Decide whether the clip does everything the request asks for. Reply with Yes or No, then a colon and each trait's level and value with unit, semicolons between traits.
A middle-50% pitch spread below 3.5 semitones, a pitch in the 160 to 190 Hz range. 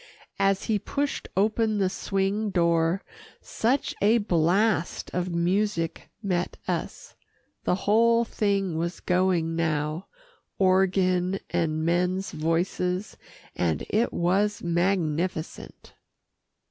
Yes: average, 3.0 semitones; medium, 185 Hz